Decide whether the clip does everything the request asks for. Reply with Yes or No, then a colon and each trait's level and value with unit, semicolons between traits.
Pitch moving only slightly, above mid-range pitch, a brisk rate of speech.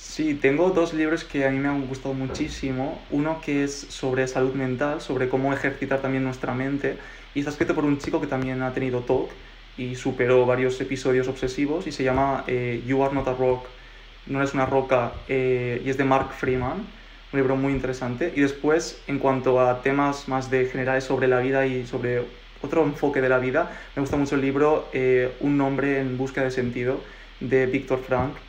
No: narrow, 1.6 semitones; low, 135 Hz; fast, 200 wpm